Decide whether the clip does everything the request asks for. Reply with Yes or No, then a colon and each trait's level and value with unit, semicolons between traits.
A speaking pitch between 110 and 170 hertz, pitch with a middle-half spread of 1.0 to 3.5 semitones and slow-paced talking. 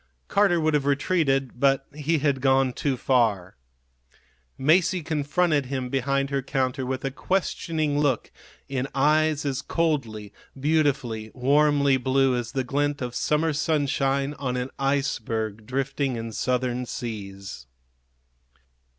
Yes: low, 135 Hz; average, 2.7 semitones; slow, 125 wpm